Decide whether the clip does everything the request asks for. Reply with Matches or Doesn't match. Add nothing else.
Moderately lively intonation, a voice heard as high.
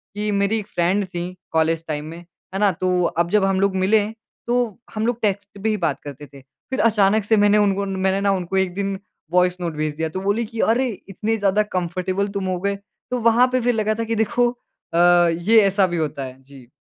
Matches